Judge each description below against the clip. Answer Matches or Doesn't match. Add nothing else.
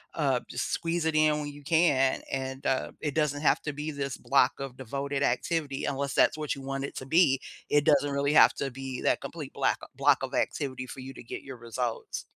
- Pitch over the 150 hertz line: Doesn't match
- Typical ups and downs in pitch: Doesn't match